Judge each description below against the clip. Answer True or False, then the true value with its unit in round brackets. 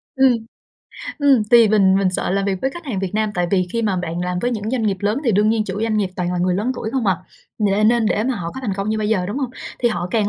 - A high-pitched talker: True (210 Hz)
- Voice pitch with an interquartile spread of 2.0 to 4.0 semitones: True (3.6 semitones)